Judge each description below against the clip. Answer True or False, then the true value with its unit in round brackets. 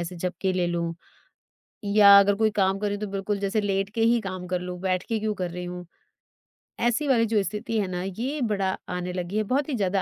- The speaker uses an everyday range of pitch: True (3.0 semitones)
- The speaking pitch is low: False (195 Hz)